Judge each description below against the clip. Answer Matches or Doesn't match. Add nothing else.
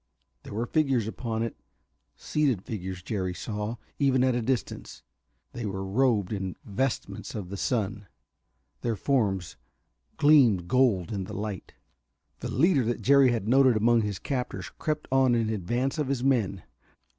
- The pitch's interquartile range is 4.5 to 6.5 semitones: Matches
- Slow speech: Doesn't match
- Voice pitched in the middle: Doesn't match